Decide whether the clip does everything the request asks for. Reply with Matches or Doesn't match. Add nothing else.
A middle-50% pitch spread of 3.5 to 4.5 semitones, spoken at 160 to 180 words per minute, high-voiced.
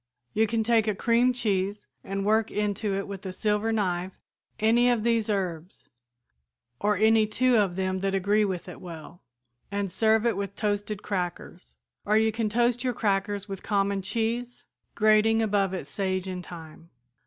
Doesn't match